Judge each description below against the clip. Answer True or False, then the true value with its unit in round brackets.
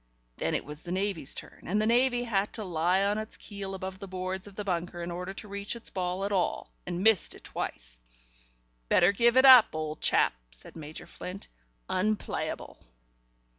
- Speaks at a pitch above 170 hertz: True (190 Hz)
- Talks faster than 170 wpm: True (190 wpm)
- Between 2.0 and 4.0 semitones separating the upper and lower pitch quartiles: True (3.0 semitones)